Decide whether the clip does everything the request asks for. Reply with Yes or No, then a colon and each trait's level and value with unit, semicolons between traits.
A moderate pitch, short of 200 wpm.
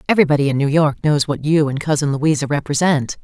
No: medium, 145 Hz; fast, 205 wpm